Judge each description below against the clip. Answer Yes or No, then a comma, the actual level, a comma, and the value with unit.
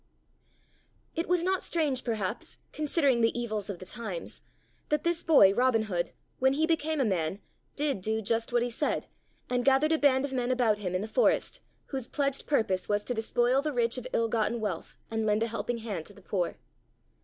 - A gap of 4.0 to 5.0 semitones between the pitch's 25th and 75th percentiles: Yes, average, 4.7 semitones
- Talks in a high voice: Yes, high, 235 Hz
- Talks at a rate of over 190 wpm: Yes, average, 200 wpm